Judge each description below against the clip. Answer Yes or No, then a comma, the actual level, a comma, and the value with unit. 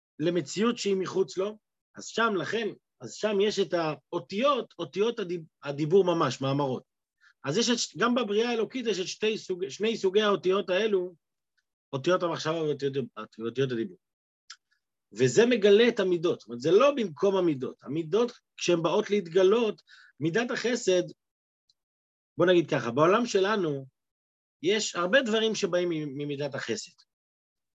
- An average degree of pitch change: No, wide, 6.2 semitones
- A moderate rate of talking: Yes, average, 130 wpm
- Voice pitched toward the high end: No, medium, 180 Hz